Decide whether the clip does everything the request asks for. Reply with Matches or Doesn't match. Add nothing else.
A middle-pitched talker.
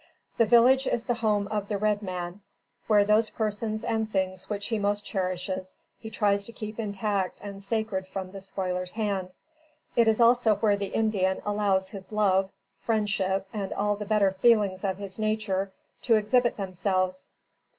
Doesn't match